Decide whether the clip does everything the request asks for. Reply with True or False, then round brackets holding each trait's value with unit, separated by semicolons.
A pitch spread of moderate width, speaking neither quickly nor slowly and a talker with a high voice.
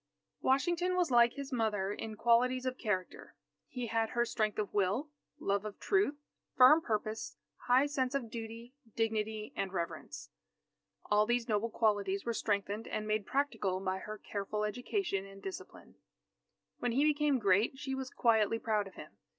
True (3.7 semitones; 160 wpm; 225 Hz)